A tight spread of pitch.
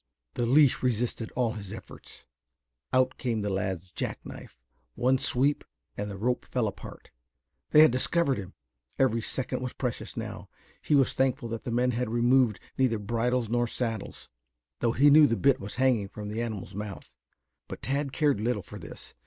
No: average, 3.1 semitones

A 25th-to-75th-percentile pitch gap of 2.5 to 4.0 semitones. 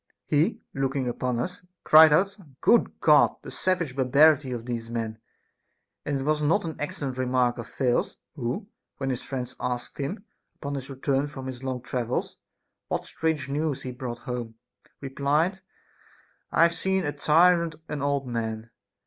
Yes: average, 3.6 semitones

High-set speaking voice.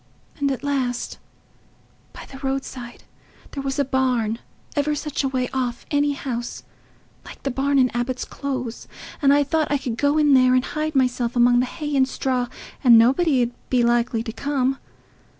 Yes: very high, 265 Hz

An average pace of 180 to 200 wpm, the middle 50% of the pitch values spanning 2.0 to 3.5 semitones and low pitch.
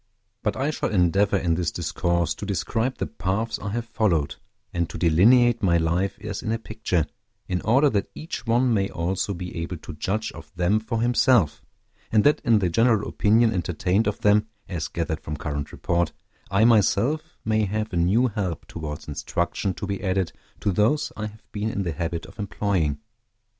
No: average, 190 wpm; average, 4.3 semitones; low, 100 Hz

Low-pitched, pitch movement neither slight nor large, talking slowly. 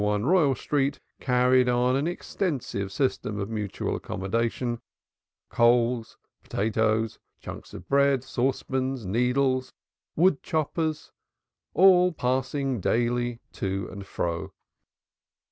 Yes: low, 125 Hz; average, 3.6 semitones; slow, 100 wpm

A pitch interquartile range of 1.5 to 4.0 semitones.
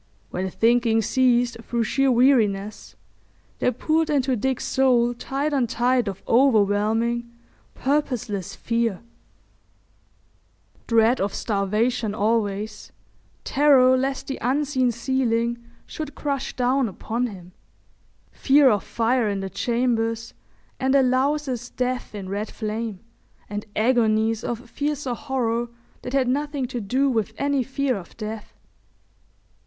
Yes: average, 3.2 semitones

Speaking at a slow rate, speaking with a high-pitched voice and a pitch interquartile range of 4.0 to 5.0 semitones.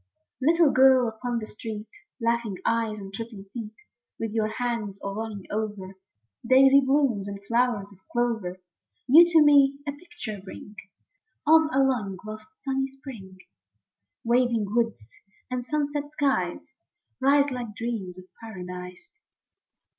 Yes: slow, 130 wpm; high, 235 Hz; average, 4.5 semitones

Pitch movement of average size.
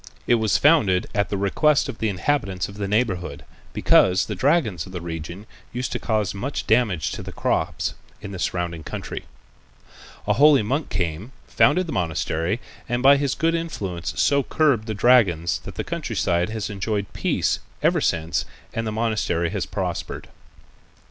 No: wide, 5.7 semitones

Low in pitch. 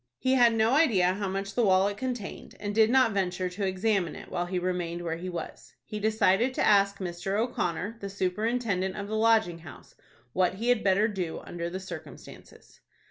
No: high, 195 Hz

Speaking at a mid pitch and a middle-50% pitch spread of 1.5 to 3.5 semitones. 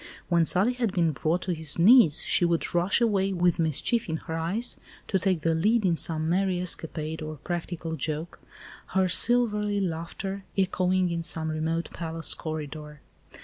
Yes: medium, 170 Hz; average, 3.0 semitones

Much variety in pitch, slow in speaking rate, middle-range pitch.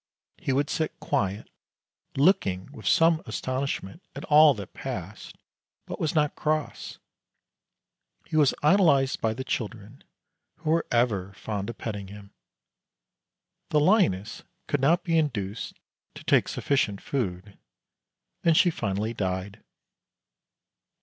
No: wide, 7.3 semitones; slow, 125 wpm; low, 130 Hz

